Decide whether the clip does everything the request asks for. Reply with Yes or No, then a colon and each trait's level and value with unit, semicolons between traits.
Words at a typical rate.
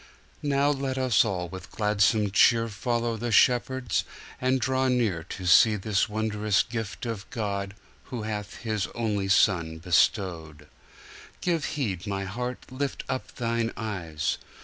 No: slow, 125 wpm